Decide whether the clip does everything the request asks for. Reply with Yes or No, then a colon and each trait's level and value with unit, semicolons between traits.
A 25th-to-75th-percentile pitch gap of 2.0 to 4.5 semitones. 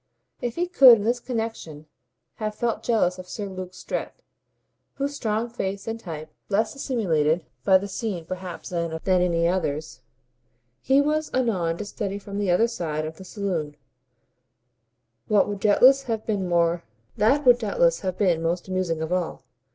No: average, 5.0 semitones